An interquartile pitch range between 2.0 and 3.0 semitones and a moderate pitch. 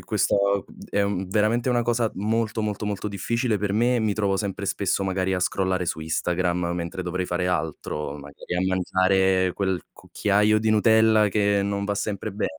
No: narrow, 2.6 semitones; low, 100 Hz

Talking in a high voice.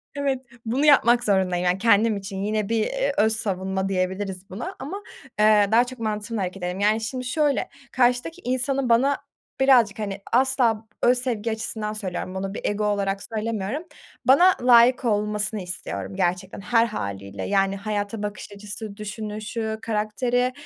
Yes: high, 215 Hz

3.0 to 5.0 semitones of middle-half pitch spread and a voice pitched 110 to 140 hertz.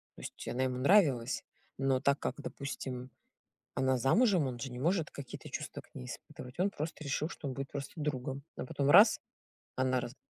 No: narrow, 2.6 semitones; low, 135 Hz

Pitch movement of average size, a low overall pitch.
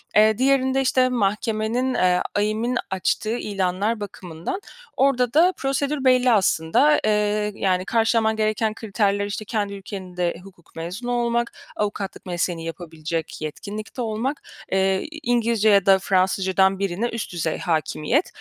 No: average, 4.1 semitones; high, 210 Hz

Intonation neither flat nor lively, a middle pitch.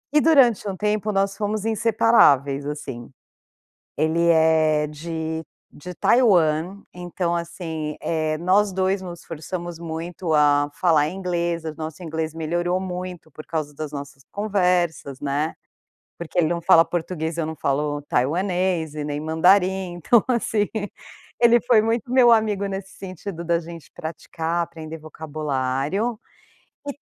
Yes: average, 3.6 semitones; medium, 170 Hz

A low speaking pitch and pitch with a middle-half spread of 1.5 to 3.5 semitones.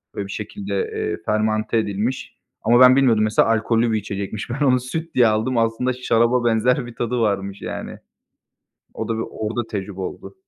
Yes: low, 115 Hz; average, 2.8 semitones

